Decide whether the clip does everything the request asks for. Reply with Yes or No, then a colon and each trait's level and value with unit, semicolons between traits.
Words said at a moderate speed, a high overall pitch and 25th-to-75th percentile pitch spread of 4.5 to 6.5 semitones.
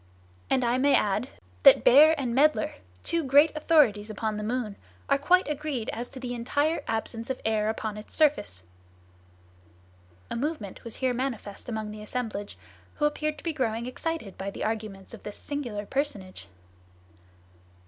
Yes: average, 165 wpm; high, 240 Hz; average, 5.3 semitones